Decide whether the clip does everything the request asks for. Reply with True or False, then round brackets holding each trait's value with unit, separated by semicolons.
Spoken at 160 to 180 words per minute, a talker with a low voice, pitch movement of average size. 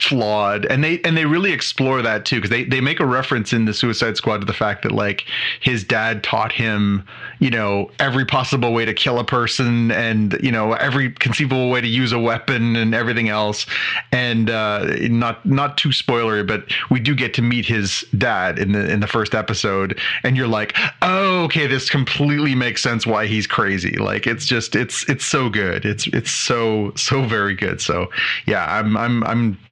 False (200 wpm; 120 Hz; 3.4 semitones)